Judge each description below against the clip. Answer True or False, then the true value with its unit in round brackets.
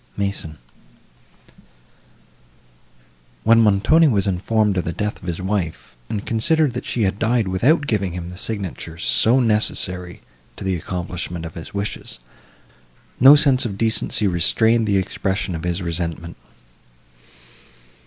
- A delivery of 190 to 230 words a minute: False (135 wpm)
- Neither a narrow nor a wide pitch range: True (4.3 semitones)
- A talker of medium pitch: False (100 Hz)